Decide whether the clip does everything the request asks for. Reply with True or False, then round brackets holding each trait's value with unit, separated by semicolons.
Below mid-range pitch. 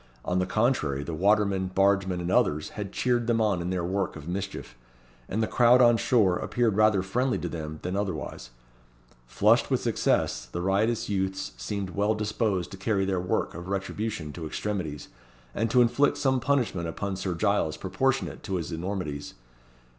True (95 Hz)